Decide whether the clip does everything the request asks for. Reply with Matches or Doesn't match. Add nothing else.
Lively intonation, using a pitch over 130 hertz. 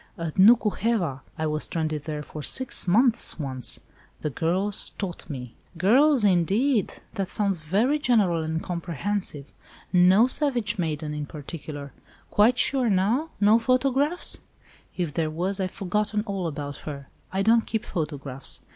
Matches